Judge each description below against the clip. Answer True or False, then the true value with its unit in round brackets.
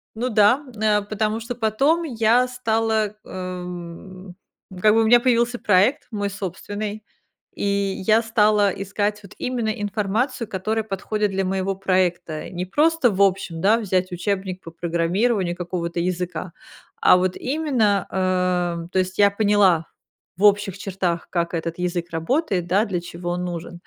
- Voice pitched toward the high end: True (200 Hz)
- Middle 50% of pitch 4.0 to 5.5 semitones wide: False (3.4 semitones)